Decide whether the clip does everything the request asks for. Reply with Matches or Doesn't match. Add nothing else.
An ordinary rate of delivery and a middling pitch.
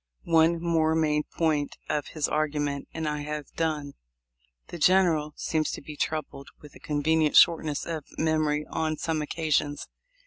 Matches